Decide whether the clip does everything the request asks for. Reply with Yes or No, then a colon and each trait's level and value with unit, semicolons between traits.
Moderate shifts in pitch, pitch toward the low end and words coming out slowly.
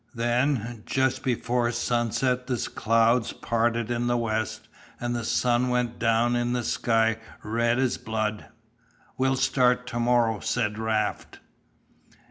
No: narrow, 1.6 semitones; low, 120 Hz; slow, 125 wpm